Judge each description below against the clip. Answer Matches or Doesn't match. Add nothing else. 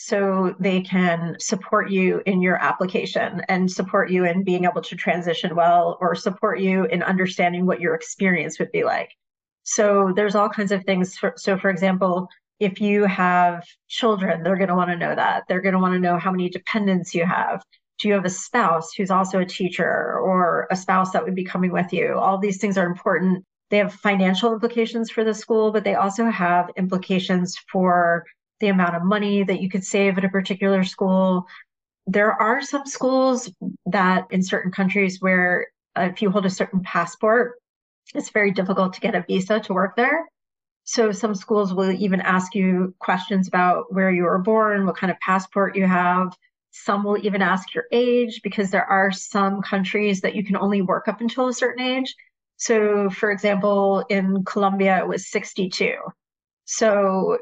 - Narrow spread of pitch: Matches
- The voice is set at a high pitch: Matches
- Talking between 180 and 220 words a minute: Matches